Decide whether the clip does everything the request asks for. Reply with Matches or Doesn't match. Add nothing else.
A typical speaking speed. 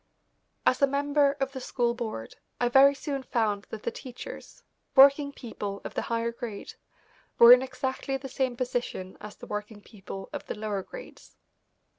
Matches